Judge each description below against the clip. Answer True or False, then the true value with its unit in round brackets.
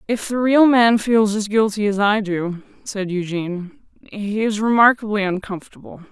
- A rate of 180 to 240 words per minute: False (155 wpm)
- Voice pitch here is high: True (210 Hz)